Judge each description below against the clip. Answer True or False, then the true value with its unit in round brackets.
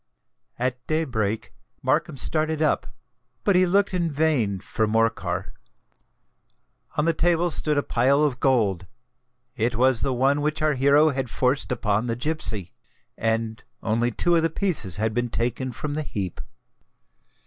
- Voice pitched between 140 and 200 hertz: False (130 Hz)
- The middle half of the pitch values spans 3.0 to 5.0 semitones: False (5.5 semitones)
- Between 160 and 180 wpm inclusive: False (150 wpm)